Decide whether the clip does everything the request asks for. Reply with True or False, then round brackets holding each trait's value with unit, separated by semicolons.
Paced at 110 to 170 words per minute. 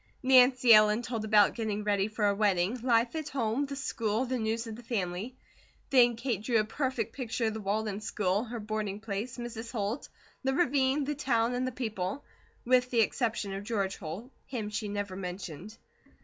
False (190 wpm)